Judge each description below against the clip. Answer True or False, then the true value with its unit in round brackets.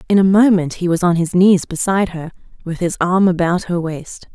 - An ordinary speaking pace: False (220 wpm)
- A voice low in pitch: False (180 Hz)